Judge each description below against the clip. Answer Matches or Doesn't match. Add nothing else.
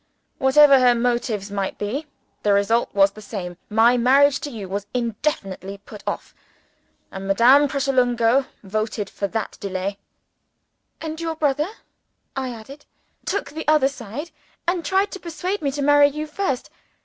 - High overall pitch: Matches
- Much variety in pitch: Matches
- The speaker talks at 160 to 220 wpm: Doesn't match